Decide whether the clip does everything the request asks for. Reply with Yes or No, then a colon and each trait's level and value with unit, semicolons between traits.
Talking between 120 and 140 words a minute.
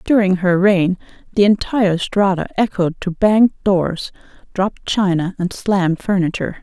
Yes: slow, 135 wpm